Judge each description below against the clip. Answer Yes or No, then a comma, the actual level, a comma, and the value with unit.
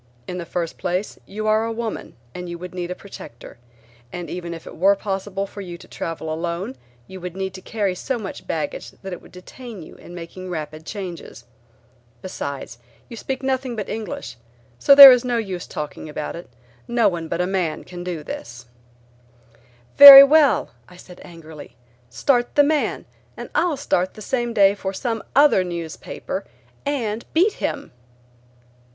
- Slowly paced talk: No, average, 175 wpm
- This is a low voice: No, high, 190 Hz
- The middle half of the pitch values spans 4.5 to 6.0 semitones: Yes, average, 5.1 semitones